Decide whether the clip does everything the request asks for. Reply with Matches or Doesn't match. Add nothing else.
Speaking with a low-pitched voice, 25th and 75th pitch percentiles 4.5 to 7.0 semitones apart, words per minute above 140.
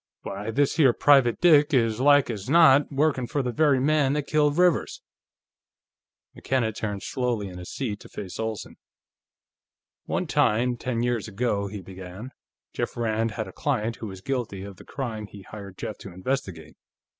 Matches